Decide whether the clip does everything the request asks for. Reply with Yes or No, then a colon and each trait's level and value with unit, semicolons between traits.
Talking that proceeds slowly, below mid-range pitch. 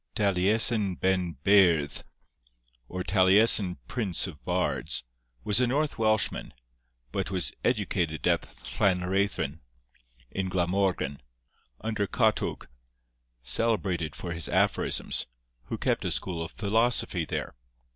Yes: slow, 105 wpm; very low, 95 Hz